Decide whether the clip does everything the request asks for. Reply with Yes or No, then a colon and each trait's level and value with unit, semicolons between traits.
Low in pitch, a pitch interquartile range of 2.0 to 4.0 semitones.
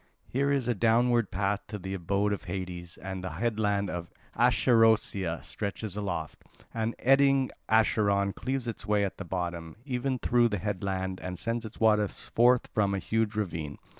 Yes: low, 105 Hz; average, 3.6 semitones